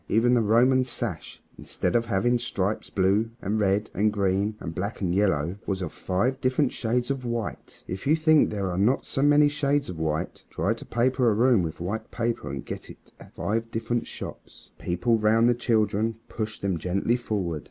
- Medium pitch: No, low, 110 Hz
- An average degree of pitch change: Yes, average, 4.0 semitones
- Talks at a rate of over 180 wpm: Yes, average, 200 wpm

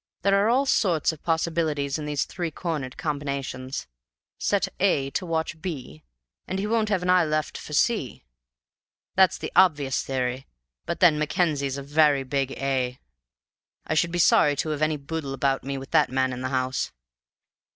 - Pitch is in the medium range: Yes, medium, 150 Hz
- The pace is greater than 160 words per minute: Yes, average, 175 wpm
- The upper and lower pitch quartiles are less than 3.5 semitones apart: No, average, 4.0 semitones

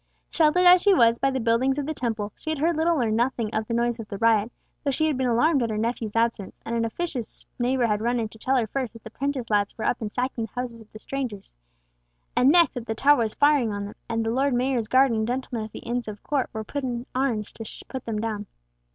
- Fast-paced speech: Yes, fast, 270 wpm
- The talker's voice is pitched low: No, high, 235 Hz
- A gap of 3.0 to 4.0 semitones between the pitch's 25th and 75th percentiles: Yes, average, 3.4 semitones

